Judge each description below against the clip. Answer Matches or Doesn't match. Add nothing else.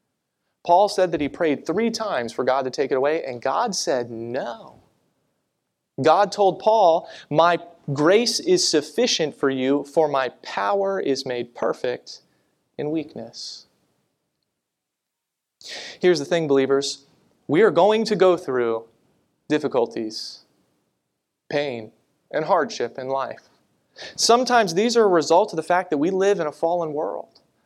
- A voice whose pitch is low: Doesn't match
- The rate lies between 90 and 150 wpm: Matches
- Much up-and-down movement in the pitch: Matches